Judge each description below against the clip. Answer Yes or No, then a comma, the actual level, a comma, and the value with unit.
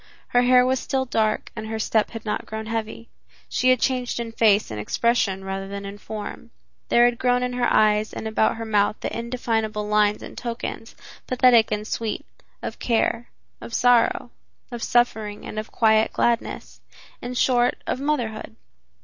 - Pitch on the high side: Yes, high, 225 Hz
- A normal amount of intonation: No, narrow, 2.3 semitones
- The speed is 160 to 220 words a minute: Yes, average, 175 wpm